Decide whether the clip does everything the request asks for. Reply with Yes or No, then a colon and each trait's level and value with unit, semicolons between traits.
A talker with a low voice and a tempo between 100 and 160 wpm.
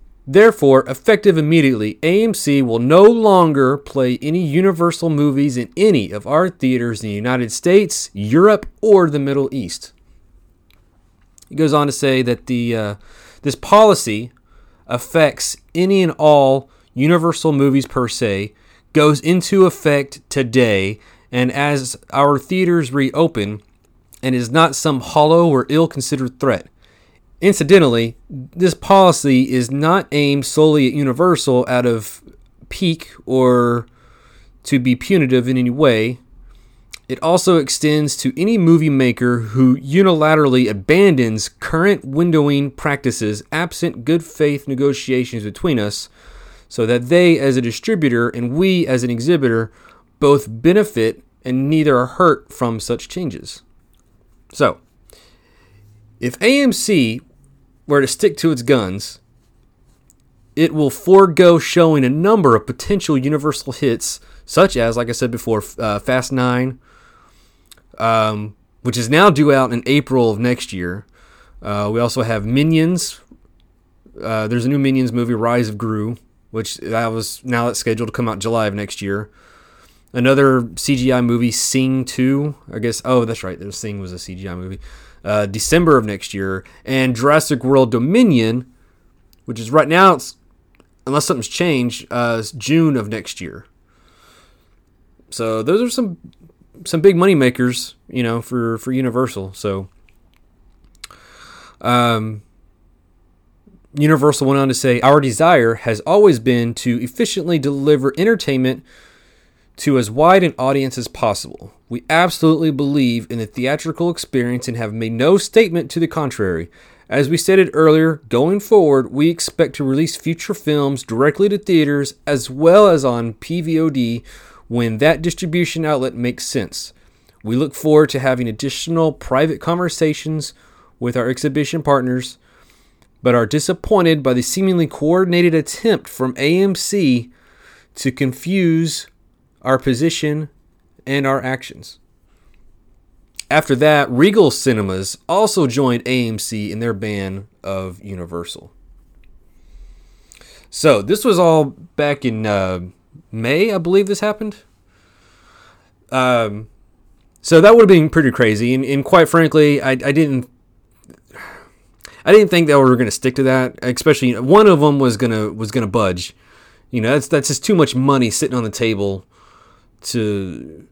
Yes: low, 130 Hz; average, 140 wpm